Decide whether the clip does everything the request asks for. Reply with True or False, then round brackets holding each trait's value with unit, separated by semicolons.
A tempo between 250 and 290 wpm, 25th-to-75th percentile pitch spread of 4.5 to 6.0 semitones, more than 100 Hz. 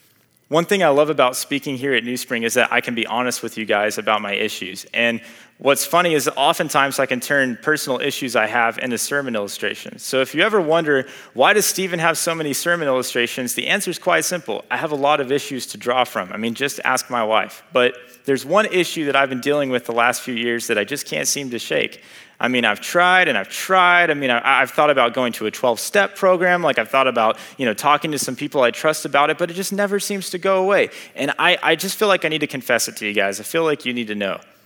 True (260 wpm; 5.2 semitones; 140 Hz)